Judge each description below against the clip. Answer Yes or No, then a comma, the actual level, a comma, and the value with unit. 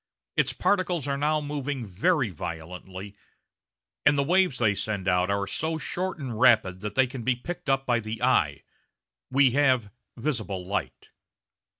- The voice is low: Yes, low, 125 Hz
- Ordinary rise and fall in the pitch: No, wide, 6.4 semitones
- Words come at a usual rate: Yes, average, 160 wpm